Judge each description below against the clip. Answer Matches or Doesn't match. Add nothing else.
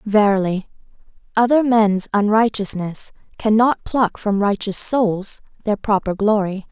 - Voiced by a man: Doesn't match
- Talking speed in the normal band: Doesn't match